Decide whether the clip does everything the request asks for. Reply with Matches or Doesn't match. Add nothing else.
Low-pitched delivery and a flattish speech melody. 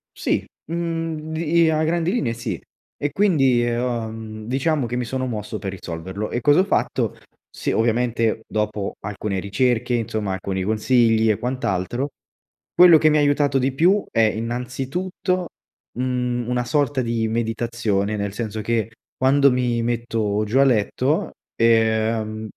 Doesn't match